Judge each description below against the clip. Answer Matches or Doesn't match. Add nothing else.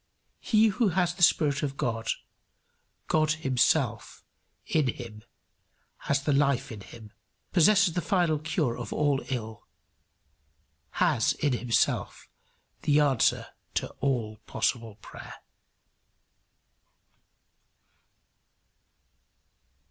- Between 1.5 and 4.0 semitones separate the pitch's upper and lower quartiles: Doesn't match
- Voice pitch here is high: Doesn't match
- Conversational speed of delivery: Doesn't match